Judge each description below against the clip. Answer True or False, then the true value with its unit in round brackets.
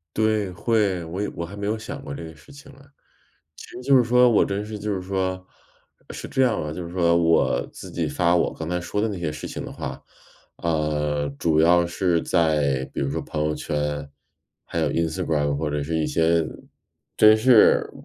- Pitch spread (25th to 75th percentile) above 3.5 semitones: True (5.0 semitones)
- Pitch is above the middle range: False (85 Hz)